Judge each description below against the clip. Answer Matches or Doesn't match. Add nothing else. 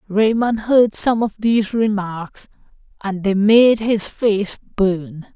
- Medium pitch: Doesn't match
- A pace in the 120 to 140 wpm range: Matches